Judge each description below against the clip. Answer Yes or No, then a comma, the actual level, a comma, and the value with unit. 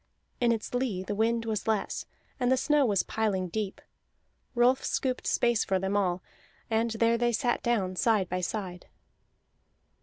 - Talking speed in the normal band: Yes, average, 160 wpm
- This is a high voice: Yes, high, 220 Hz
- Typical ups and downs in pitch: Yes, average, 3.7 semitones